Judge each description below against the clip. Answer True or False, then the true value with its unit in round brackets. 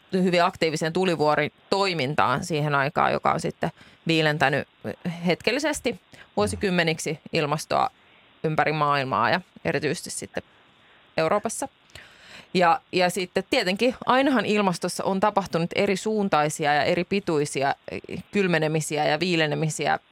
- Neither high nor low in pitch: True (175 Hz)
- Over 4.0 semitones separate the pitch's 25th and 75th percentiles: True (4.5 semitones)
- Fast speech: False (105 wpm)